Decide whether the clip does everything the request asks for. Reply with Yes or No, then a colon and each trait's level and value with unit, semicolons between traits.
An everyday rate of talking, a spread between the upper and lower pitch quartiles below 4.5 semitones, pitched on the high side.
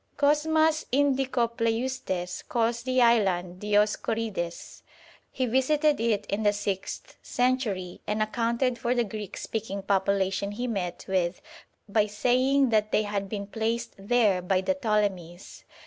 No: slow, 130 wpm; average, 3.8 semitones; high, 220 Hz